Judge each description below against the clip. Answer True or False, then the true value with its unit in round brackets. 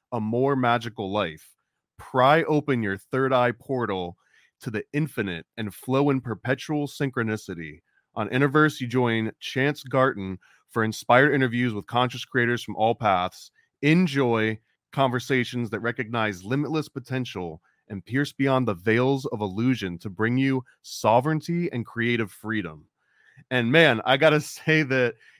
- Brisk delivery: False (140 wpm)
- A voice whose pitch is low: True (125 Hz)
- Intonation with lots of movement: False (3.7 semitones)